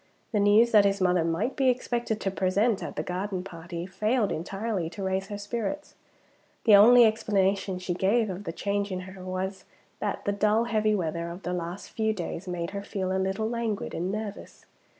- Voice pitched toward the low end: No, high, 200 Hz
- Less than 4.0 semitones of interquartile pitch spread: Yes, average, 2.7 semitones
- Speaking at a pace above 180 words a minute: Yes, average, 200 wpm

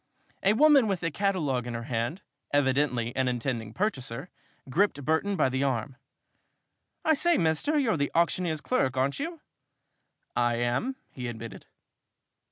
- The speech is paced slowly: No, average, 145 wpm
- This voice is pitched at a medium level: Yes, medium, 145 Hz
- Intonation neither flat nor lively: No, wide, 8.2 semitones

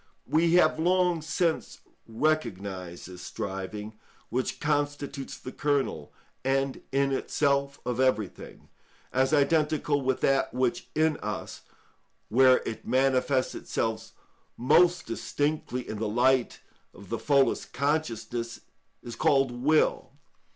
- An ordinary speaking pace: No, slow, 115 wpm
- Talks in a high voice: No, low, 135 Hz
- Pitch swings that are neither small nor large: Yes, average, 4.3 semitones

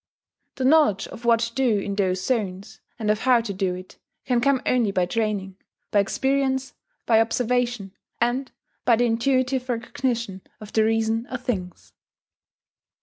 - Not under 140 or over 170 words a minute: Yes, average, 155 wpm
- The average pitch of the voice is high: Yes, high, 230 Hz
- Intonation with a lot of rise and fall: No, average, 3.8 semitones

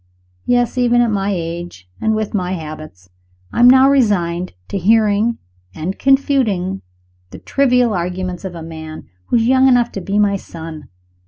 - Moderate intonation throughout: No, wide, 5.8 semitones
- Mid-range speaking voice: No, high, 200 Hz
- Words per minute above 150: Yes, average, 165 wpm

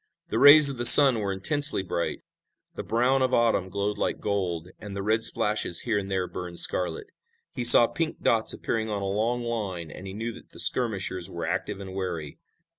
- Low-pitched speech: Yes, low, 105 Hz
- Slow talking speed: No, average, 200 wpm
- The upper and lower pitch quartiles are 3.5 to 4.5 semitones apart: Yes, average, 4.1 semitones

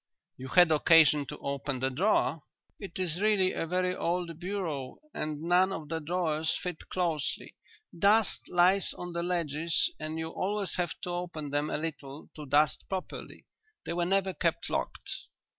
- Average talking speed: Yes, average, 165 wpm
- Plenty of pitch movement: No, average, 3.1 semitones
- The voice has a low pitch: No, medium, 170 Hz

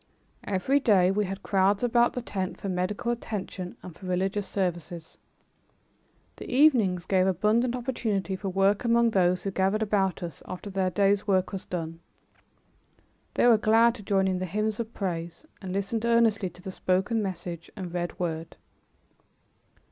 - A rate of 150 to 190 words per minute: Yes, average, 165 wpm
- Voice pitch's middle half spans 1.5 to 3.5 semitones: Yes, average, 2.9 semitones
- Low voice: No, high, 195 Hz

